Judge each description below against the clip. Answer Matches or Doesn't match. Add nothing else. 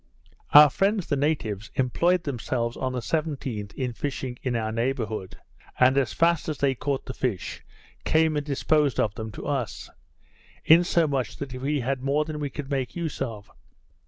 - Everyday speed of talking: Matches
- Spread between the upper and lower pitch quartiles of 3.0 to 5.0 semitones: Matches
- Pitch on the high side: Doesn't match